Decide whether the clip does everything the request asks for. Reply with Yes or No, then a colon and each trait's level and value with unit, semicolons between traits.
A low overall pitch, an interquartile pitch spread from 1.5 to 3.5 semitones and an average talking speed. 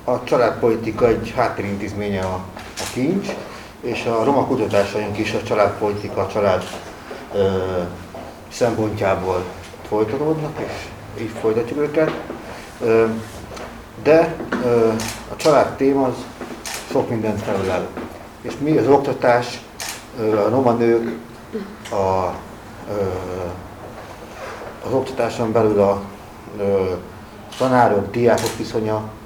No: low, 110 Hz; average, 2.7 semitones; slow, 90 wpm